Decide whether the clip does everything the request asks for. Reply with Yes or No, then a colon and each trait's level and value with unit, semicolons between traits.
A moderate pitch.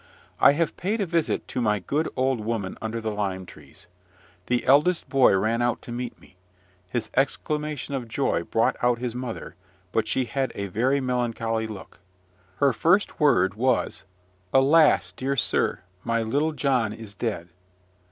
No: low, 125 Hz